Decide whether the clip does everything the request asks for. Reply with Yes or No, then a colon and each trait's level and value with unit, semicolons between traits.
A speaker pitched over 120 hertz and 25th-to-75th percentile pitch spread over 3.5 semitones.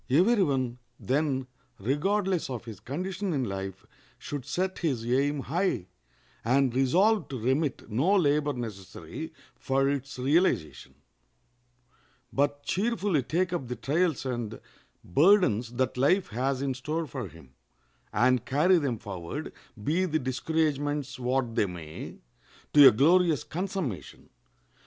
Yes: medium, 140 Hz; average, 5.3 semitones